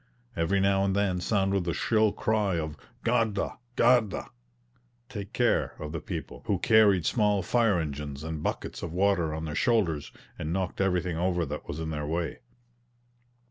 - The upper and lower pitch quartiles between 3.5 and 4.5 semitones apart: Yes, average, 4.2 semitones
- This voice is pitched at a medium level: No, very low, 95 Hz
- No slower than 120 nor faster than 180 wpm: Yes, average, 170 wpm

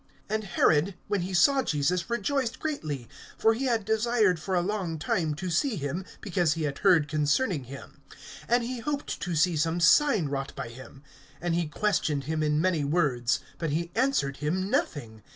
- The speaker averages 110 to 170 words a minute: No, average, 185 wpm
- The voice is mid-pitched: Yes, medium, 175 Hz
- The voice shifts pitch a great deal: Yes, wide, 6.3 semitones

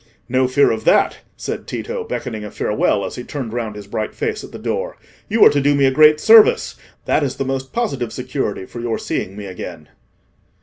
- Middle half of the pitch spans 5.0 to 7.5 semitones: Yes, wide, 5.6 semitones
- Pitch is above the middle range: No, low, 130 Hz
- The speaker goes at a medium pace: No, fast, 210 wpm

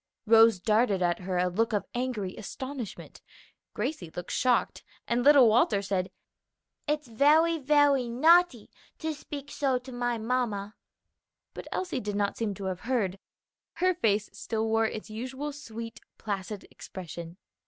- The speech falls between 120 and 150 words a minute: Yes, average, 145 wpm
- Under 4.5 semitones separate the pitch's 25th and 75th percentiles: No, average, 4.9 semitones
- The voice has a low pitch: No, high, 230 Hz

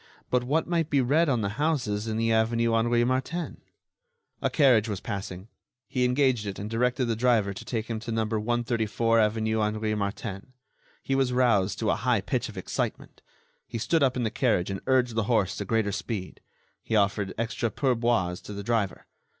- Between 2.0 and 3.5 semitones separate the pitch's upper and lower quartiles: Yes, average, 3.0 semitones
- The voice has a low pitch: Yes, low, 115 Hz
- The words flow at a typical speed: Yes, average, 190 wpm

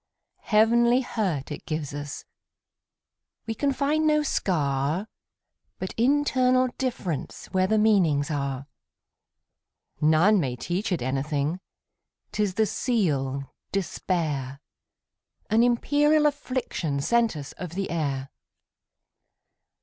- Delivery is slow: Yes, slow, 85 wpm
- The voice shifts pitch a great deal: Yes, wide, 8.6 semitones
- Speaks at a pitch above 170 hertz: Yes, medium, 185 Hz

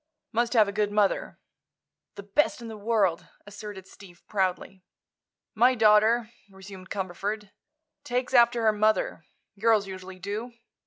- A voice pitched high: Yes, high, 210 Hz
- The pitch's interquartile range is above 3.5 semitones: No, average, 2.8 semitones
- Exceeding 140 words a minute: No, slow, 135 wpm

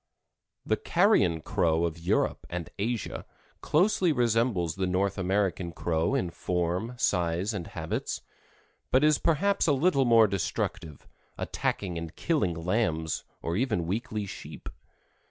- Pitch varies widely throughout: Yes, wide, 5.9 semitones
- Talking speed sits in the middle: No, slow, 130 wpm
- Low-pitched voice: Yes, very low, 95 Hz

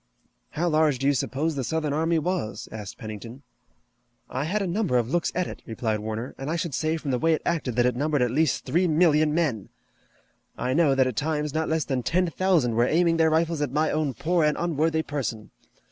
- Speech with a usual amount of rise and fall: Yes, average, 4.4 semitones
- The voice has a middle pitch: Yes, medium, 150 Hz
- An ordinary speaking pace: No, fast, 220 wpm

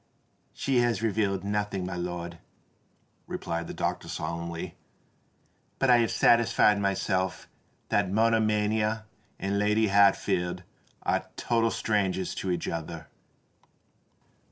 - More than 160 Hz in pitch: No, low, 100 Hz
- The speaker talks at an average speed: No, slow, 105 wpm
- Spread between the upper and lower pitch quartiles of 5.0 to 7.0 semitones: No, average, 3.6 semitones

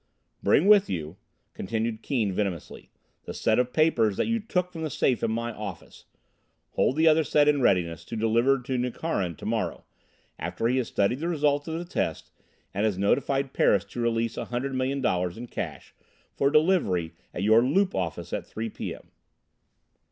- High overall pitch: No, low, 120 Hz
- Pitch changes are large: Yes, wide, 6.3 semitones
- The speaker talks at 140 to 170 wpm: No, average, 185 wpm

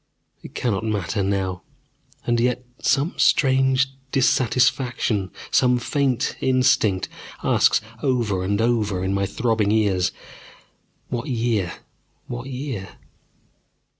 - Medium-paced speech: No, slow, 105 wpm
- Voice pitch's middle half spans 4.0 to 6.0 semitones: Yes, average, 4.4 semitones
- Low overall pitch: Yes, low, 115 Hz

